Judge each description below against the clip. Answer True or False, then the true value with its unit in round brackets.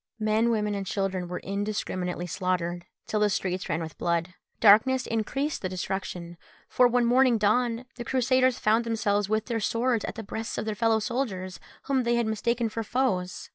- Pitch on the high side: True (215 Hz)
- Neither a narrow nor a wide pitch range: True (4.0 semitones)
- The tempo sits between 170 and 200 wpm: True (180 wpm)